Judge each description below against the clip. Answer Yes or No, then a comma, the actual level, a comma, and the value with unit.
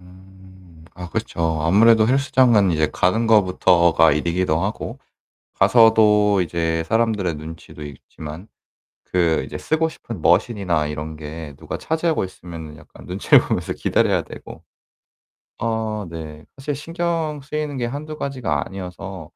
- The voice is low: Yes, very low, 95 Hz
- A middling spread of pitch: No, wide, 6.0 semitones